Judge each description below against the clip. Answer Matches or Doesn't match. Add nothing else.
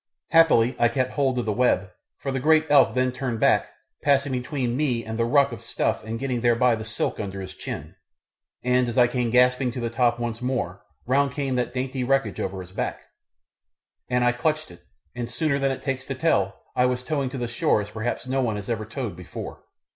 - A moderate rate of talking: Doesn't match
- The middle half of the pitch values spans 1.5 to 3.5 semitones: Matches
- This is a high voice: Doesn't match